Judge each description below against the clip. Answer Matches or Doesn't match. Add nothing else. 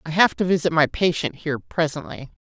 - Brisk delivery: Doesn't match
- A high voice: Doesn't match